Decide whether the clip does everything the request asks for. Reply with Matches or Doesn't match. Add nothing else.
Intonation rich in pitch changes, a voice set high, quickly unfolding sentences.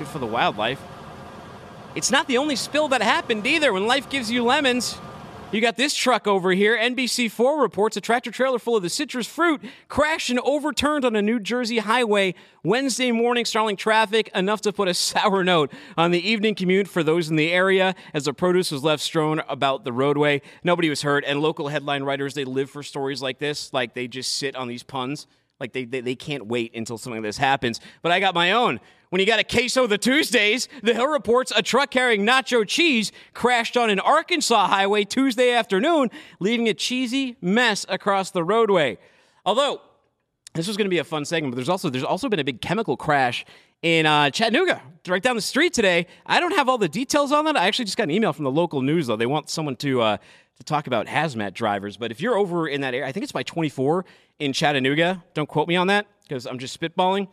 Matches